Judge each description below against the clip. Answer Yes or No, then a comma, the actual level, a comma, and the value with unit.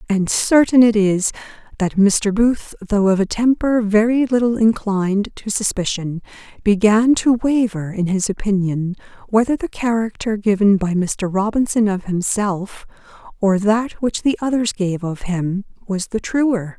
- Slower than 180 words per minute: Yes, average, 150 wpm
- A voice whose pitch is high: Yes, high, 210 Hz